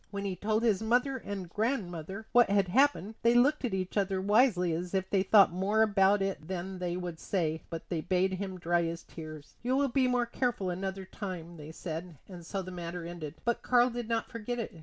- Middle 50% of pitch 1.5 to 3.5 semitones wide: No, average, 4.4 semitones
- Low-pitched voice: No, high, 190 Hz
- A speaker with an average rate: No, fast, 220 wpm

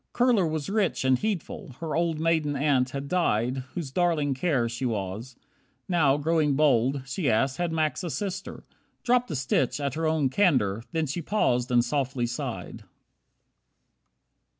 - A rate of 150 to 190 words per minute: Yes, average, 155 wpm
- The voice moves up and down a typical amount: Yes, average, 4.6 semitones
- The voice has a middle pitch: Yes, medium, 145 Hz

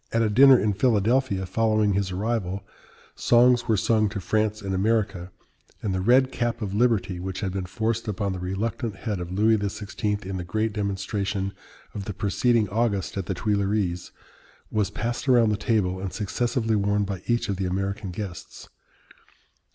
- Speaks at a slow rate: No, average, 175 wpm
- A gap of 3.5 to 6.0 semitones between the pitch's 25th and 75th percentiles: No, average, 2.8 semitones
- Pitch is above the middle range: No, low, 105 Hz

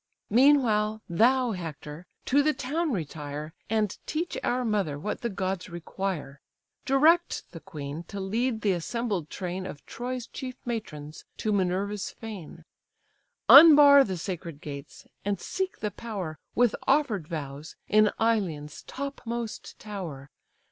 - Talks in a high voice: Yes, high, 205 Hz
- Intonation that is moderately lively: No, wide, 6.7 semitones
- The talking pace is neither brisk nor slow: No, slow, 130 wpm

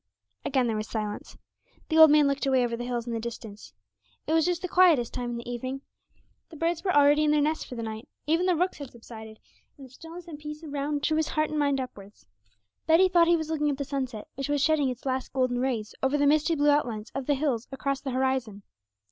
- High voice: Yes, very high, 275 Hz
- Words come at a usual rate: No, fast, 240 wpm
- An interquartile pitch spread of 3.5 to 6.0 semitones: Yes, average, 4.1 semitones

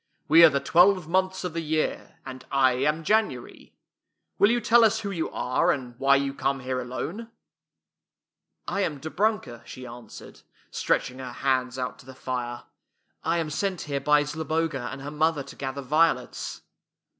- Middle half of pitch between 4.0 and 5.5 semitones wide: Yes, average, 4.4 semitones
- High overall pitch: No, medium, 145 Hz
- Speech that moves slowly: No, average, 185 wpm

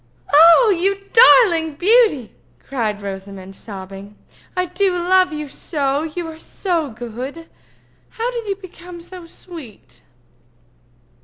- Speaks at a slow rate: Yes, slow, 110 wpm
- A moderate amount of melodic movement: No, wide, 8.2 semitones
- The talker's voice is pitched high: Yes, very high, 325 Hz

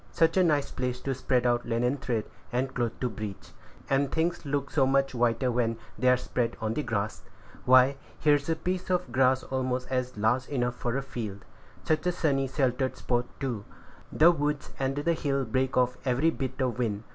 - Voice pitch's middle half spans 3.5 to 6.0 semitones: No, narrow, 2.5 semitones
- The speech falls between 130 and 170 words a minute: No, average, 195 wpm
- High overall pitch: No, low, 130 Hz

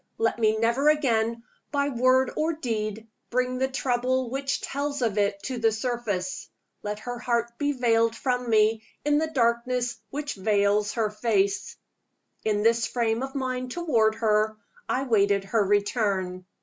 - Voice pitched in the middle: No, high, 235 Hz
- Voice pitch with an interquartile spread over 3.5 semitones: No, average, 3.2 semitones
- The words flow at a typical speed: Yes, average, 155 wpm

